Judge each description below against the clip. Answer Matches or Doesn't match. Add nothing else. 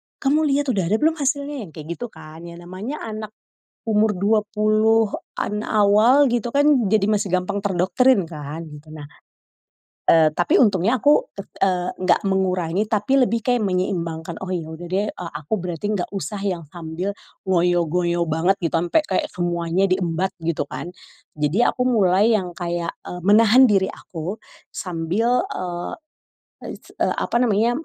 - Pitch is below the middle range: Doesn't match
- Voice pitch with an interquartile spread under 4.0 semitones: Doesn't match